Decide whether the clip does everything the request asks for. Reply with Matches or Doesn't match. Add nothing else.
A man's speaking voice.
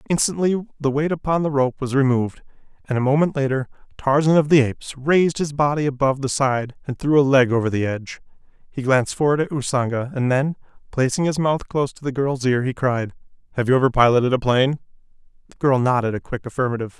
Matches